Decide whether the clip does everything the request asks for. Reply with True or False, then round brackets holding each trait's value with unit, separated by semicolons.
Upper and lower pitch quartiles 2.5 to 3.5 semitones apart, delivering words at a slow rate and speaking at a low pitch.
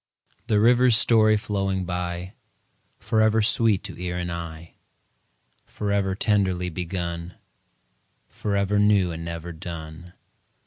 True (3.2 semitones; 105 wpm; 95 Hz)